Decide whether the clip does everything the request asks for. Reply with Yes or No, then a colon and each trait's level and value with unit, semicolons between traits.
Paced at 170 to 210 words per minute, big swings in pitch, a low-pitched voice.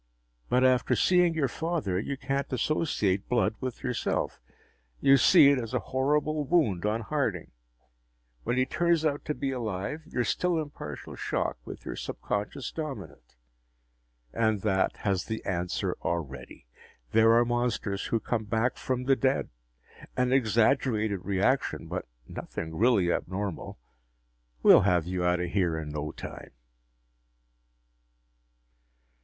No: average, 140 wpm; wide, 6.1 semitones; low, 115 Hz